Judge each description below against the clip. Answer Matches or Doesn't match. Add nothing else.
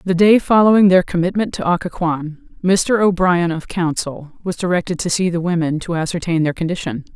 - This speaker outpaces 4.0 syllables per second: Matches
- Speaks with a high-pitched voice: Doesn't match